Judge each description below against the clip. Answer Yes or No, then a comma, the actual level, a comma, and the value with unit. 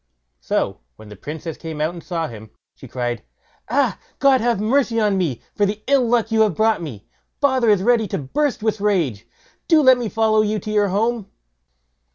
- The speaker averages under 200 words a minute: No, fast, 205 wpm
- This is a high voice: Yes, high, 210 Hz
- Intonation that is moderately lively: No, wide, 6.3 semitones